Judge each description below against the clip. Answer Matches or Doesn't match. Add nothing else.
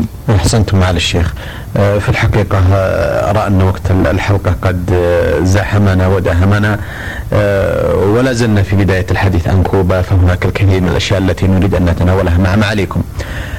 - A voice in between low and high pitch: Doesn't match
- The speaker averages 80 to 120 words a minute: Doesn't match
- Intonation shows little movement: Matches